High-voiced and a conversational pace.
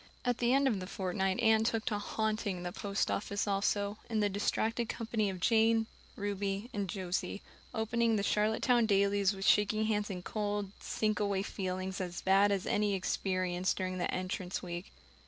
Yes: high, 205 Hz; average, 170 wpm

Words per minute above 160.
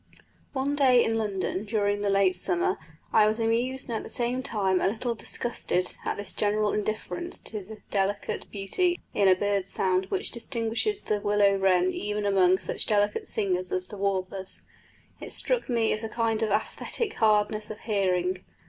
Yes: average, 175 wpm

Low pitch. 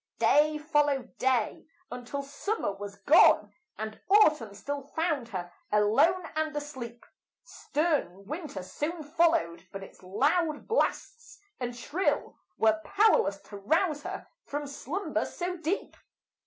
No: very high, 290 Hz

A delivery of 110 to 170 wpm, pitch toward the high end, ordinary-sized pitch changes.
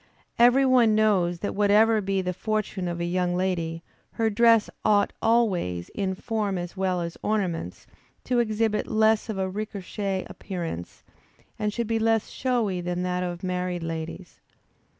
Yes: average, 155 wpm; high, 195 Hz; average, 3.5 semitones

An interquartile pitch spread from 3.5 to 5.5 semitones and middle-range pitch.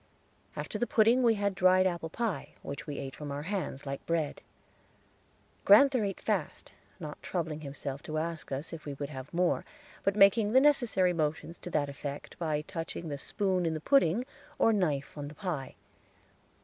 Yes: average, 5.2 semitones; medium, 165 Hz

